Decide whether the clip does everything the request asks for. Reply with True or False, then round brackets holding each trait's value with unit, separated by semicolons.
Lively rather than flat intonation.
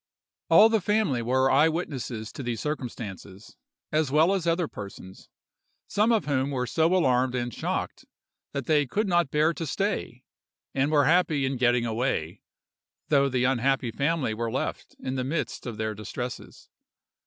False (4.8 semitones)